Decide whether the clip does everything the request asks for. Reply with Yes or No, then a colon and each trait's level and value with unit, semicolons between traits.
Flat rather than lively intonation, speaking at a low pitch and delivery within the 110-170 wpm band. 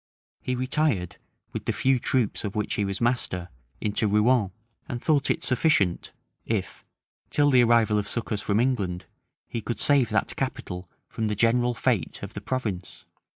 No: average, 3.9 semitones; low, 115 Hz; average, 165 wpm